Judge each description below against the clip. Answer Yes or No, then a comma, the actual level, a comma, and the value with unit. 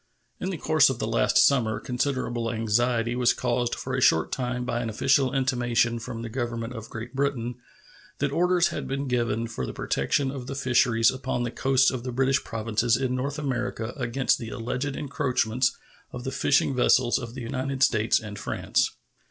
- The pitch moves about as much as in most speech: No, narrow, 2.3 semitones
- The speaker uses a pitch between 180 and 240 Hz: No, low, 125 Hz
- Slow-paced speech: No, average, 185 wpm